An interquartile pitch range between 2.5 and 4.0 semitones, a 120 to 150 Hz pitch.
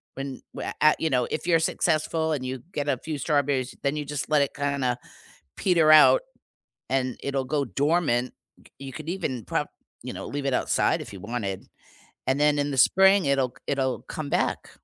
Yes: average, 2.9 semitones; medium, 140 Hz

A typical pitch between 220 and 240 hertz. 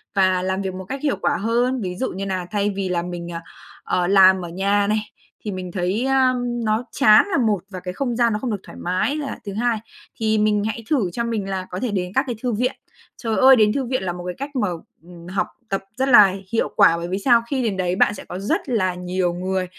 No: high, 205 Hz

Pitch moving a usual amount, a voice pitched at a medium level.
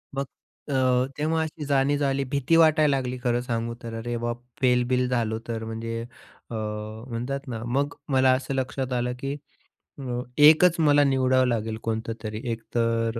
No: average, 3.1 semitones; low, 125 Hz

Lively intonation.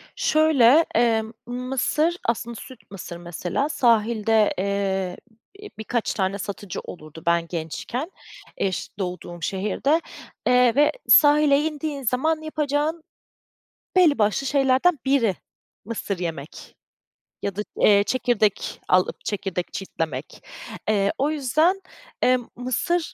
Yes: wide, 6.8 semitones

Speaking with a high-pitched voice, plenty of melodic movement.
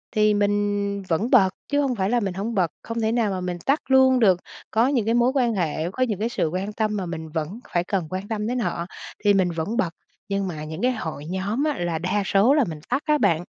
No: high, 205 Hz; average, 4.7 semitones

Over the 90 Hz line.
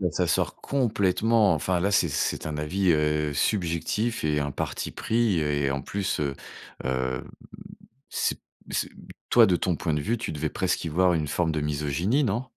No: very low, 85 Hz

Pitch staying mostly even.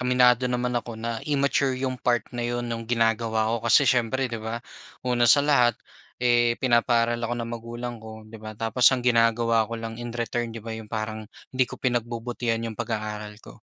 Yes: narrow, 1.5 semitones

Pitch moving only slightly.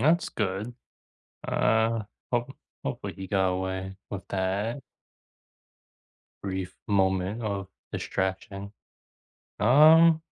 No: average, 3.7 semitones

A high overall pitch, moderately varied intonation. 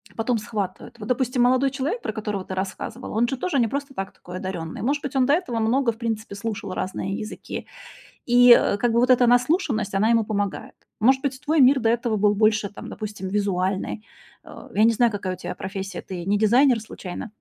Yes: high, 225 Hz; average, 3.8 semitones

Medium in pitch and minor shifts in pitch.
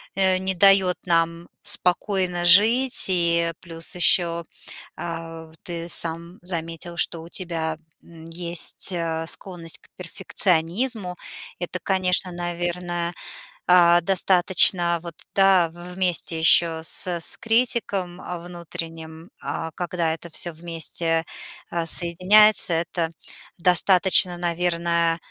Yes: medium, 175 Hz; narrow, 1.5 semitones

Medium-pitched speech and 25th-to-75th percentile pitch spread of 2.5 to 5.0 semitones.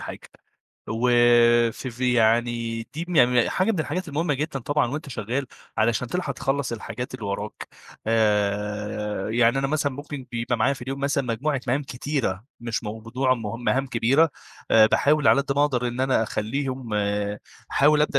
No: low, 125 Hz; average, 3.6 semitones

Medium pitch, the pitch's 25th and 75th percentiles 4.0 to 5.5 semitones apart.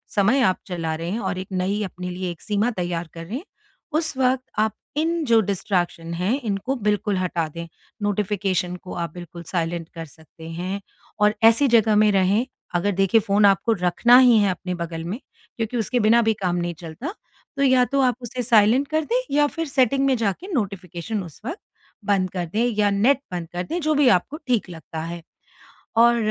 No: high, 205 Hz; average, 5.2 semitones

